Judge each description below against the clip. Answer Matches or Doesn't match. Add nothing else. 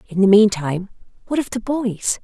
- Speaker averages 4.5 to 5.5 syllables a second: Matches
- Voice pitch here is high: Matches